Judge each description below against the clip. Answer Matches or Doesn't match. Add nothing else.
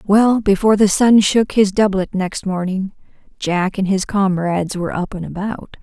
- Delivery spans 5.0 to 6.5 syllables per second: Doesn't match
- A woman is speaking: Matches